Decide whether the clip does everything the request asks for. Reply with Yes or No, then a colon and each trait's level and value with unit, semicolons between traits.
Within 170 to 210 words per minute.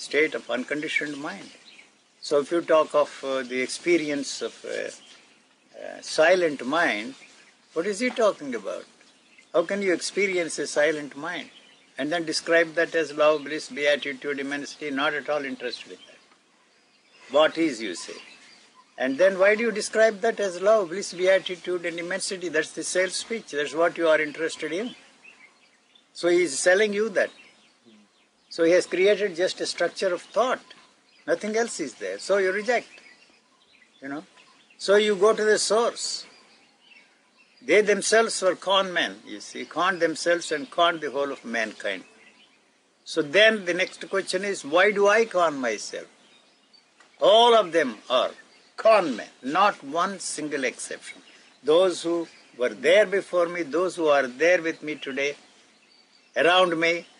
No: average, 160 wpm